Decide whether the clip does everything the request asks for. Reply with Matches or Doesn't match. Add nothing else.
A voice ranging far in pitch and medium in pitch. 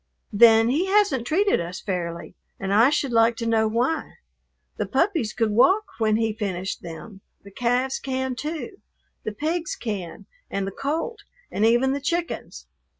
Doesn't match